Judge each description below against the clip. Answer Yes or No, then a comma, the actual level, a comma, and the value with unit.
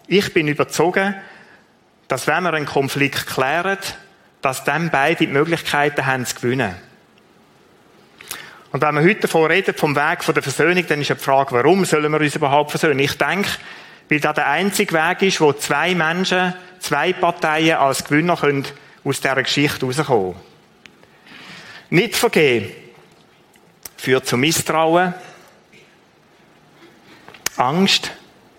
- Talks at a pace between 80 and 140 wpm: Yes, average, 135 wpm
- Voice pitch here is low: No, medium, 155 Hz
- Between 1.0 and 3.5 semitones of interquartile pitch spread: No, average, 3.9 semitones